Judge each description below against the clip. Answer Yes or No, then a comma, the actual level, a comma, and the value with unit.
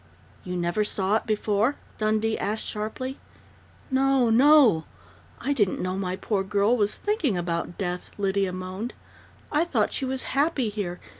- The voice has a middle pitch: No, high, 210 Hz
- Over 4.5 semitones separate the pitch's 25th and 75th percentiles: Yes, average, 5.3 semitones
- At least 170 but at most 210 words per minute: No, average, 150 wpm